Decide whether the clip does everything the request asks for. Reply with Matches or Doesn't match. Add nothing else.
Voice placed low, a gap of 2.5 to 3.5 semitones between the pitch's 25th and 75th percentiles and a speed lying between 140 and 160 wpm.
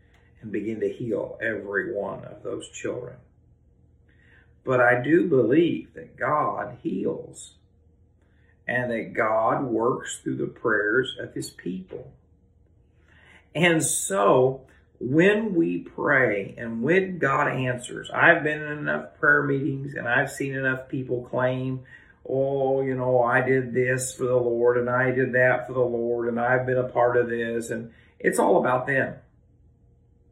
Matches